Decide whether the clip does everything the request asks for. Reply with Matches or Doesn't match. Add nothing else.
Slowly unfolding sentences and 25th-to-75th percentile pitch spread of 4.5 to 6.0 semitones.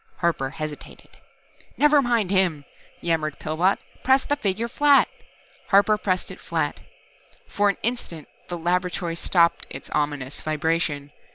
Matches